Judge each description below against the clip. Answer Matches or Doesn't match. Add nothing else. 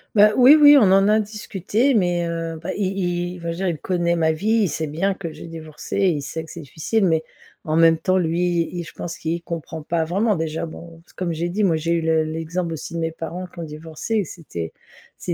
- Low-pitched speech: Doesn't match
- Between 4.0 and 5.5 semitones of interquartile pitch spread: Doesn't match